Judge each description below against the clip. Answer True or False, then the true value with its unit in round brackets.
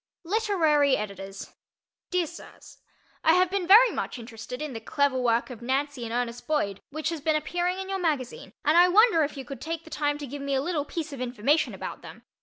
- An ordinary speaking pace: False (215 wpm)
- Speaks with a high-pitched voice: True (290 Hz)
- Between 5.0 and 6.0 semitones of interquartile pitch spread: True (5.3 semitones)